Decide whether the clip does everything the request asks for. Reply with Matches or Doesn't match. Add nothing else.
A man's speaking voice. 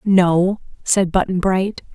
Doesn't match